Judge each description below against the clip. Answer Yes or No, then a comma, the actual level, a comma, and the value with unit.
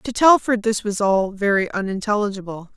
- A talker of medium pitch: No, high, 205 Hz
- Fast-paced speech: No, average, 150 wpm